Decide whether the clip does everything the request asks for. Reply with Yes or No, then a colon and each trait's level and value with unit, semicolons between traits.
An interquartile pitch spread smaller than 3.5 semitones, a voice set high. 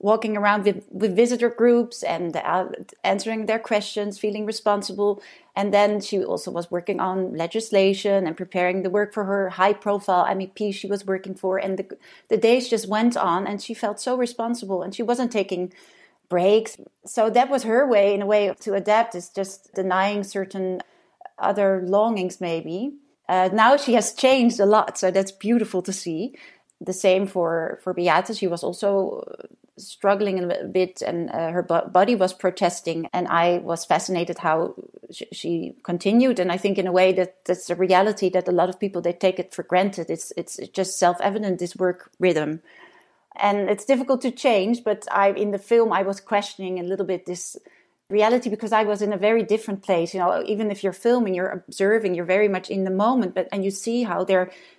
Yes: average, 2.9 semitones; high, 195 Hz